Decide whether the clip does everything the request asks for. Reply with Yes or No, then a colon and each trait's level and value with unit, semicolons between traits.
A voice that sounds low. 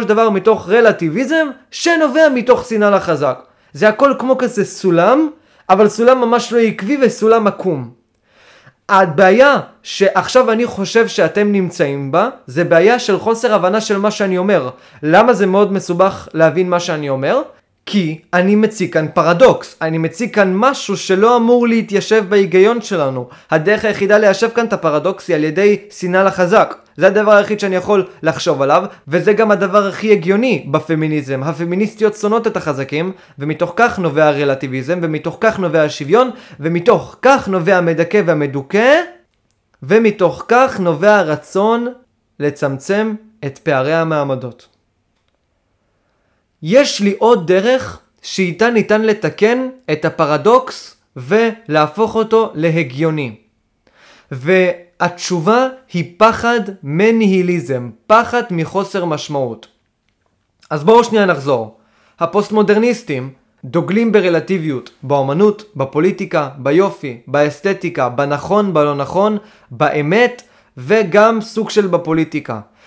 No: high, 190 Hz